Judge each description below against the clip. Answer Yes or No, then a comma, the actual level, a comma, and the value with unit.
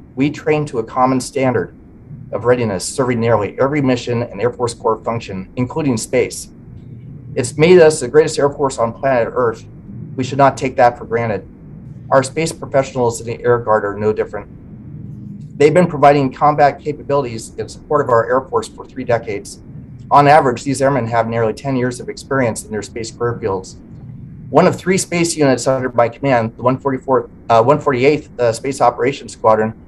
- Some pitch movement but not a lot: Yes, average, 3.4 semitones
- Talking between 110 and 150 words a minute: No, average, 185 wpm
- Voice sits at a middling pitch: No, low, 130 Hz